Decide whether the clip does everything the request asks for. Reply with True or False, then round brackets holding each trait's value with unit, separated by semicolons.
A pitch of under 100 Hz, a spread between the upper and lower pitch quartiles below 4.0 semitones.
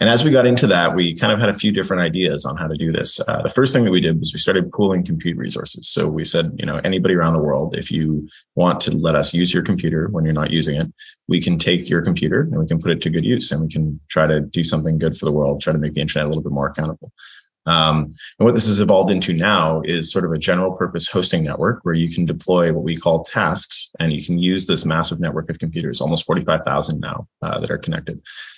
True (85 Hz; 2.5 semitones)